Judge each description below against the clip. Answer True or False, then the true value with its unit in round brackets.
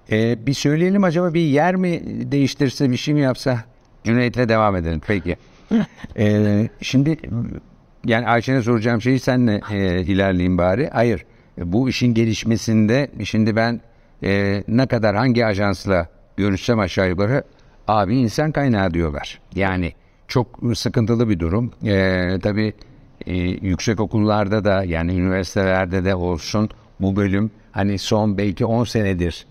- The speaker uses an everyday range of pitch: True (4.3 semitones)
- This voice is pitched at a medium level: False (110 Hz)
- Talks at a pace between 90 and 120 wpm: False (135 wpm)